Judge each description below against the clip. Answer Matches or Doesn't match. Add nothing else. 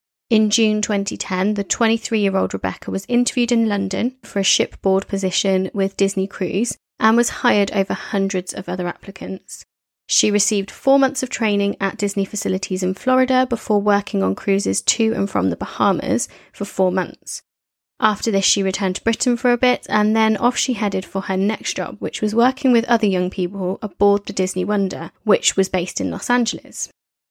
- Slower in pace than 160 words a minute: Doesn't match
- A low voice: Doesn't match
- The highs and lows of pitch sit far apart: Doesn't match